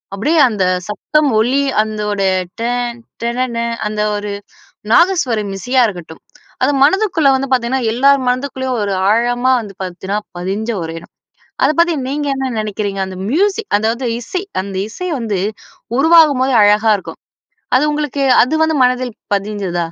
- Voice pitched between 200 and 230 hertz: No, high, 245 Hz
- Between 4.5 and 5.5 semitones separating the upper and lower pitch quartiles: Yes, average, 5.0 semitones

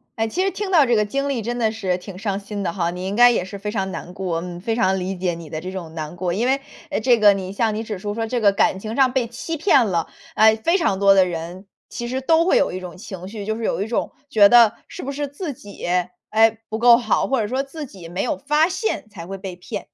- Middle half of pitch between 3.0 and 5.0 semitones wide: Yes, average, 4.6 semitones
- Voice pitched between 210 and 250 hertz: Yes, high, 215 Hz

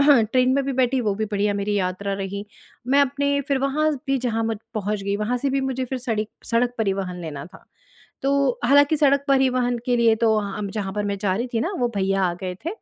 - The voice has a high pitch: Yes, high, 235 Hz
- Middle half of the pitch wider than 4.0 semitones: Yes, average, 5.1 semitones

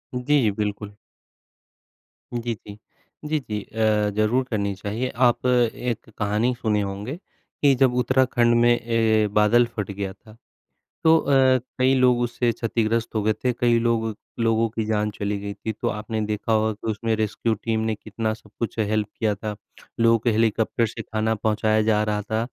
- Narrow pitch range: Yes, narrow, 1.9 semitones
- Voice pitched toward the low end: Yes, low, 110 Hz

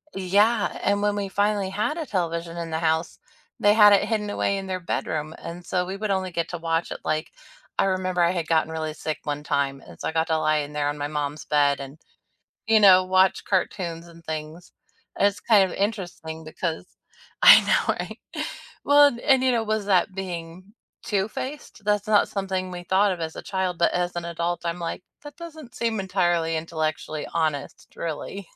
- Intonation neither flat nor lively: Yes, average, 3.9 semitones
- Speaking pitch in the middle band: Yes, medium, 180 Hz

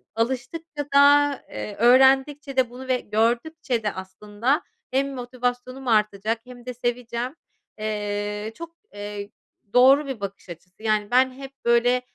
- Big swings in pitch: No, average, 3.9 semitones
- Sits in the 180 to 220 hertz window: No, high, 245 Hz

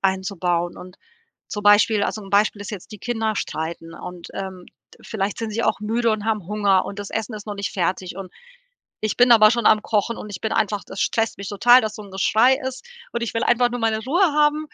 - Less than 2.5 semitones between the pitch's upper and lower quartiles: No, average, 2.8 semitones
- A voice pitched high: Yes, high, 210 Hz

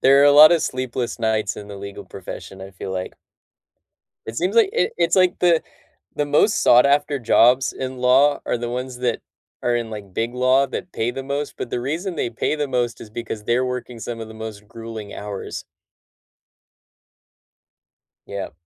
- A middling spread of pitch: Yes, average, 4.2 semitones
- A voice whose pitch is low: Yes, low, 125 Hz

